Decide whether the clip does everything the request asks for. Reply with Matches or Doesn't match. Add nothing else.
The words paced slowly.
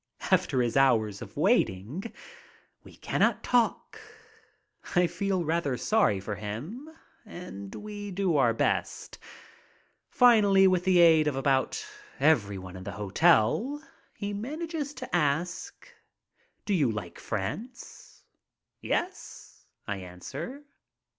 Matches